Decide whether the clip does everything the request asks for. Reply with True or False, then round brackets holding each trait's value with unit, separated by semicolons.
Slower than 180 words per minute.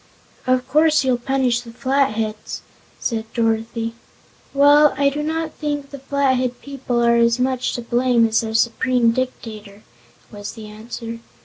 True (145 wpm)